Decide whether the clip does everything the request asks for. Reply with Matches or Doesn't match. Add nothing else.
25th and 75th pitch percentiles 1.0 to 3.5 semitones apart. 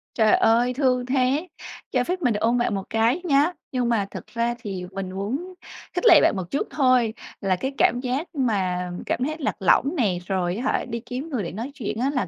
Doesn't match